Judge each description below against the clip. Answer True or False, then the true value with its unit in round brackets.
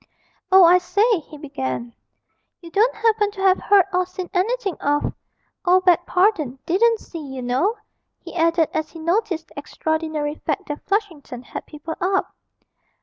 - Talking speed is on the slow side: False (160 wpm)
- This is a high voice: True (350 Hz)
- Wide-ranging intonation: False (4.5 semitones)